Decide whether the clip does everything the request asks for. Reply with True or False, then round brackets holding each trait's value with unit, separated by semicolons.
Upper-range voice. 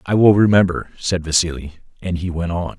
False (90 Hz)